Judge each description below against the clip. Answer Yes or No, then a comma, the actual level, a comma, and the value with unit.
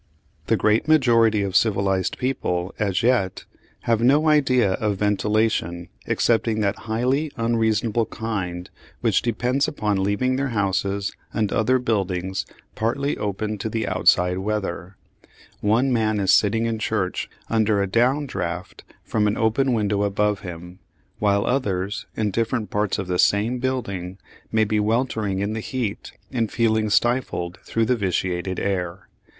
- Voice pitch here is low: Yes, low, 105 Hz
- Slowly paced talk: No, average, 145 wpm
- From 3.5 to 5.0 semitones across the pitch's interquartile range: No, average, 3.1 semitones